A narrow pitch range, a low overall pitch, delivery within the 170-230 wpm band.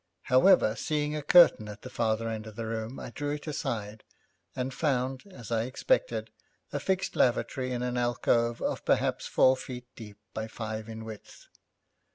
No: average, 3.3 semitones; low, 120 Hz; average, 175 wpm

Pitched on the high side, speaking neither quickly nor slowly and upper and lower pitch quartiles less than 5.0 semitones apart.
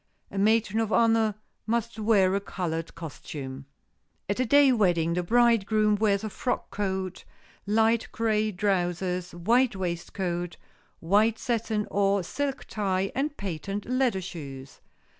No: high, 200 Hz; slow, 130 wpm; average, 4.0 semitones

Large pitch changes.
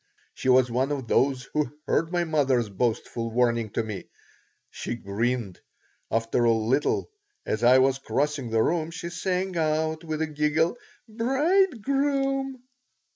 Yes: wide, 6.5 semitones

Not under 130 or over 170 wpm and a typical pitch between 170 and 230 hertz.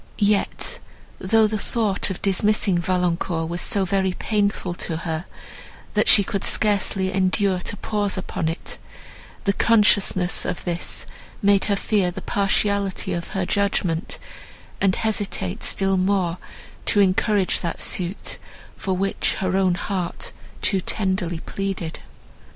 Yes: slow, 135 wpm; high, 190 Hz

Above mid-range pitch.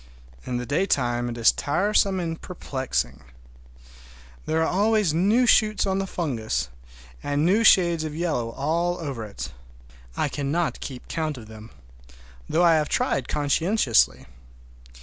No: medium, 155 Hz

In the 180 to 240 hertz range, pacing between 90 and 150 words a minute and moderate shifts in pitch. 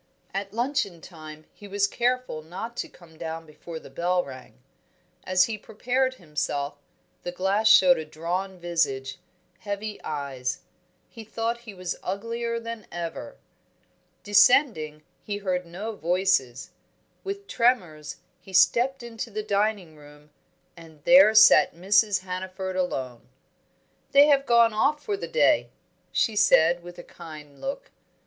No: high, 190 Hz; average, 140 wpm; wide, 5.9 semitones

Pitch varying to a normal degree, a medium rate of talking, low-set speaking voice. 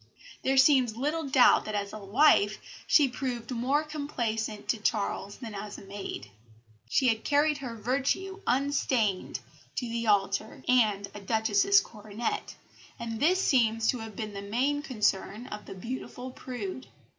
No: average, 4.2 semitones; average, 155 wpm; high, 235 Hz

